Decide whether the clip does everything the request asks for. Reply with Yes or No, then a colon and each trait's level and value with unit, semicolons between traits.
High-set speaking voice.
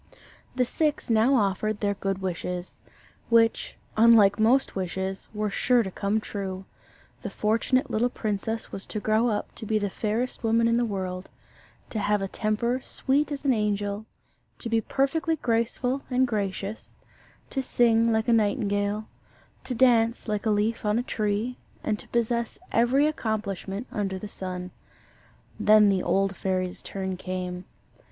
Yes: high, 215 Hz